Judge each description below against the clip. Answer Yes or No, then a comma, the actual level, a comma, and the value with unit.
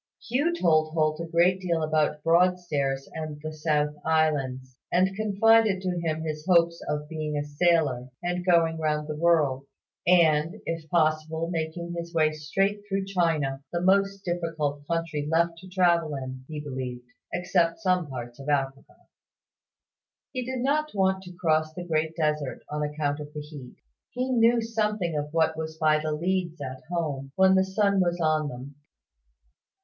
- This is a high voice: No, medium, 160 Hz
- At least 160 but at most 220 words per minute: Yes, average, 170 wpm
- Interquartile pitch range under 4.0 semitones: Yes, average, 3.1 semitones